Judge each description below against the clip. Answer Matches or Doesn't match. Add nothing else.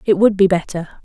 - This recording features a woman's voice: Matches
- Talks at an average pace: Doesn't match